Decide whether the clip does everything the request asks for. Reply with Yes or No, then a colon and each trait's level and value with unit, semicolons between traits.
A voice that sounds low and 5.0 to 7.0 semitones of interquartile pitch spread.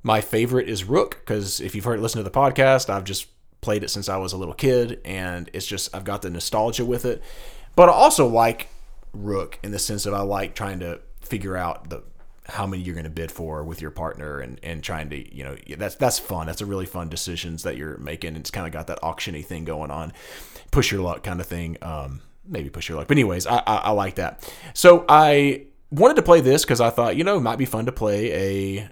Yes: very low, 95 Hz; average, 5.3 semitones